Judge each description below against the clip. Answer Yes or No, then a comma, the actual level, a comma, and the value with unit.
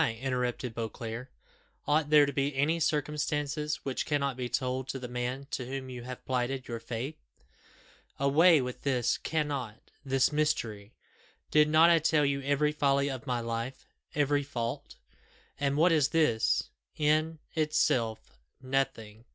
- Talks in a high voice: No, low, 135 Hz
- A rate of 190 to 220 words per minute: No, average, 145 wpm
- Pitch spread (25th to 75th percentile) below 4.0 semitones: Yes, average, 3.2 semitones